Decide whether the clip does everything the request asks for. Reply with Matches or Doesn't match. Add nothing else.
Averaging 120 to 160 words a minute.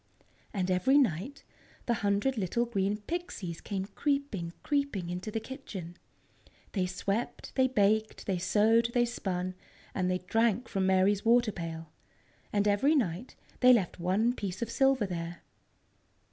Matches